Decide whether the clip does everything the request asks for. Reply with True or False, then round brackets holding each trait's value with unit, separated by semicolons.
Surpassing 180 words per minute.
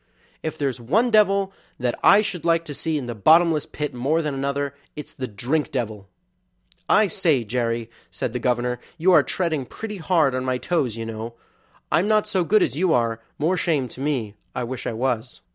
True (200 wpm)